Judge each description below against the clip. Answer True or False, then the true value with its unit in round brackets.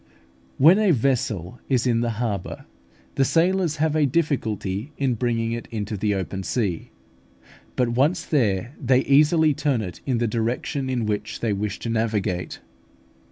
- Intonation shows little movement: False (4.8 semitones)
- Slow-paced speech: False (160 wpm)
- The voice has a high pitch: False (120 Hz)